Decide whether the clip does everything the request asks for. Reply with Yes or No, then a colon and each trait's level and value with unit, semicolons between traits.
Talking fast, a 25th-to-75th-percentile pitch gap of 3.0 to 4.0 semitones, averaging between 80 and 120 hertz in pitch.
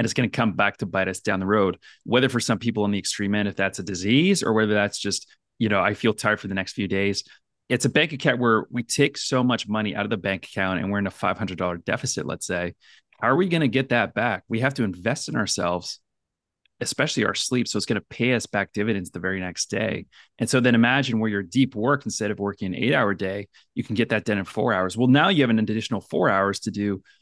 Yes: fast, 275 wpm; average, 3.5 semitones; low, 105 Hz